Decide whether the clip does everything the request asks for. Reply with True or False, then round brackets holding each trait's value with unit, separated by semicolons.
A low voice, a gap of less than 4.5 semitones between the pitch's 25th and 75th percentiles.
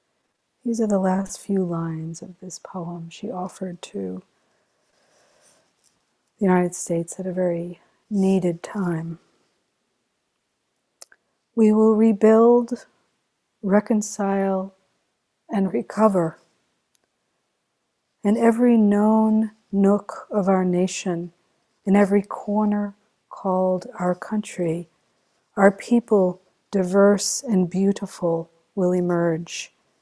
False (195 Hz; 2.9 semitones)